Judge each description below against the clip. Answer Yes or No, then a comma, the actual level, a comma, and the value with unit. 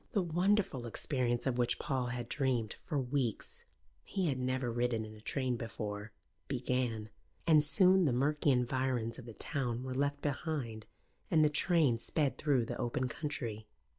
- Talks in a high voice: No, low, 130 Hz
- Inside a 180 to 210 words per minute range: No, average, 165 wpm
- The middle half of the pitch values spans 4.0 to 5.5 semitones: No, average, 3.6 semitones